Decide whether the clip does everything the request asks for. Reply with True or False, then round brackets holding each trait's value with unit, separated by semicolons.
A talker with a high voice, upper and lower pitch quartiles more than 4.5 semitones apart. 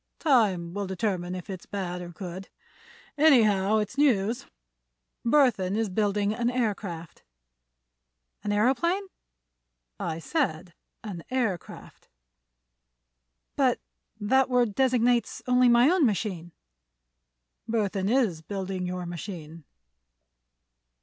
True (205 Hz; 5.1 semitones)